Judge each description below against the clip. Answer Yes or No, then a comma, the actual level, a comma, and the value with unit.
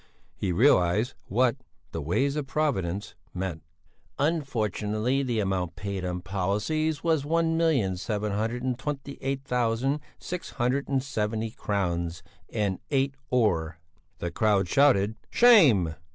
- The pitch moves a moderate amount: No, wide, 6.4 semitones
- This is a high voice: No, low, 115 Hz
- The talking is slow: Yes, slow, 120 wpm